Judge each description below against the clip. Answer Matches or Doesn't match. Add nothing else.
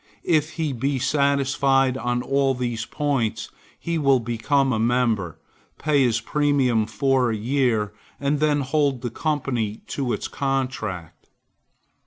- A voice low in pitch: Matches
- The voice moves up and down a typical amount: Matches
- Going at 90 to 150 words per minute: Matches